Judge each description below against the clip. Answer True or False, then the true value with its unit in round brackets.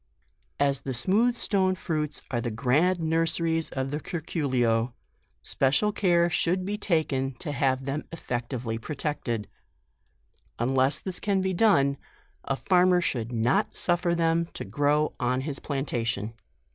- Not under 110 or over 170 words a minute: True (140 wpm)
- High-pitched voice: False (150 Hz)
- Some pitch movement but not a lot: True (4.9 semitones)